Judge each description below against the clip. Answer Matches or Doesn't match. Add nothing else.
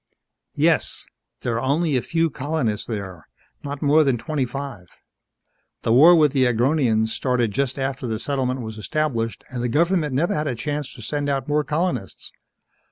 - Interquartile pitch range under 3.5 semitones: Doesn't match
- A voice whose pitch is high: Doesn't match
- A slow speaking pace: Doesn't match